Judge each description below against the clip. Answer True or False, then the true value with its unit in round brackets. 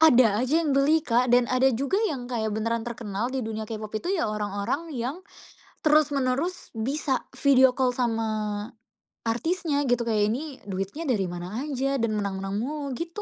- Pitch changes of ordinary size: True (4.7 semitones)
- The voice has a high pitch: True (250 Hz)